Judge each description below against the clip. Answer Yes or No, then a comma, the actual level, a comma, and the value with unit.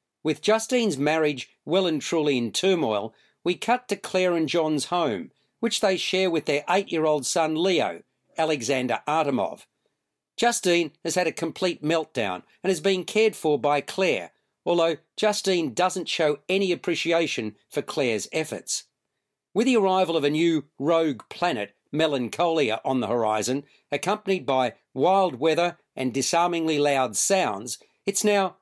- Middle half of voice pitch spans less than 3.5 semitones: No, average, 4.4 semitones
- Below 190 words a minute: Yes, average, 150 wpm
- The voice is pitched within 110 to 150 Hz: No, medium, 165 Hz